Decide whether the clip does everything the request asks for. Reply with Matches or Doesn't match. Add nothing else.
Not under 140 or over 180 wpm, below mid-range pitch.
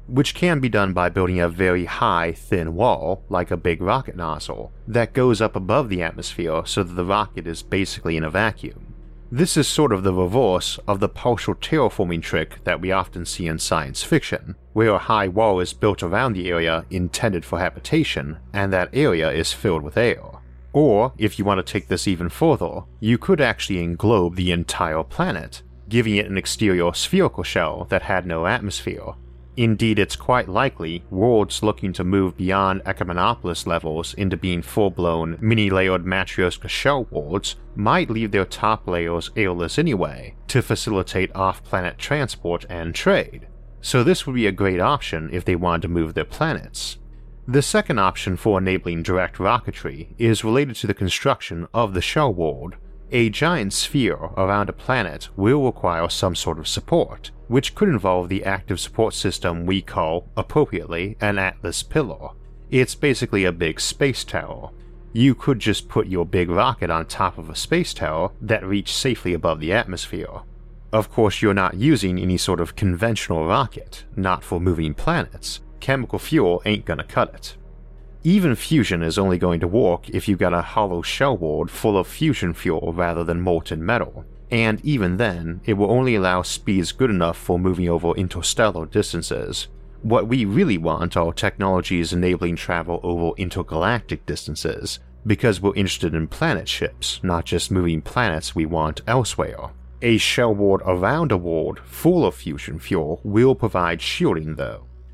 Matches